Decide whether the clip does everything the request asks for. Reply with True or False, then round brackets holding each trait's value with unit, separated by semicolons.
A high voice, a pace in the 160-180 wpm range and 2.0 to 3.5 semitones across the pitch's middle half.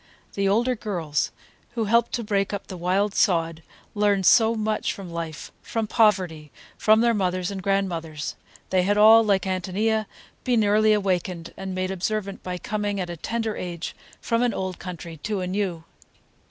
True (195 Hz; 170 wpm; 3.1 semitones)